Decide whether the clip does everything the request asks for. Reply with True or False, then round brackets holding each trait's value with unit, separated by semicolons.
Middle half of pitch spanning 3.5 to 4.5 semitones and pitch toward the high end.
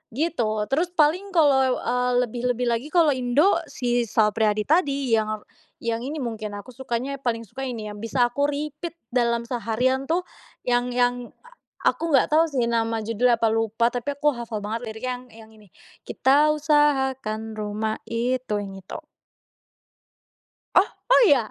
True (3.9 semitones; 245 Hz)